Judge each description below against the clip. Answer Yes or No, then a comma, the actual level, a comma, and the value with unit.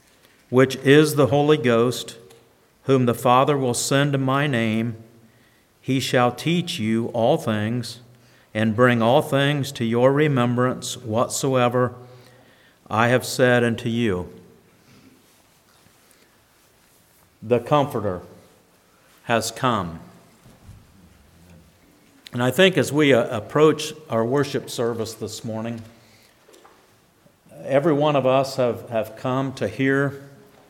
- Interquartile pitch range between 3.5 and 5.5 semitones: No, average, 3.0 semitones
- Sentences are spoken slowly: Yes, slow, 110 wpm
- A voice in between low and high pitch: No, low, 120 Hz